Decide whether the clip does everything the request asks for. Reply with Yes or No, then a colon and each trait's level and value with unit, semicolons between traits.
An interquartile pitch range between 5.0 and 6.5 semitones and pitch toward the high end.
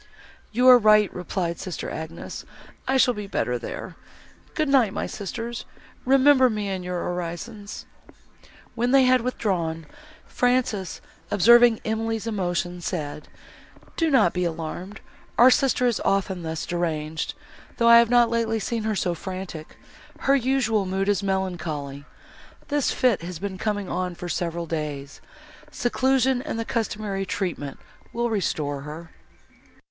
Yes: wide, 5.5 semitones; high, 200 Hz